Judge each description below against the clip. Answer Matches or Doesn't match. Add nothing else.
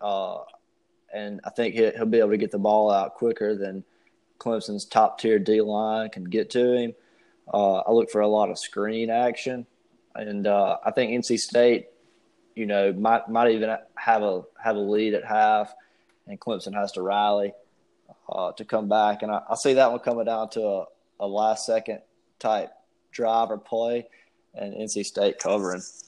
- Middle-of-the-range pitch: Doesn't match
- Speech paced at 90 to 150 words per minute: Doesn't match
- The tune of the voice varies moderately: Doesn't match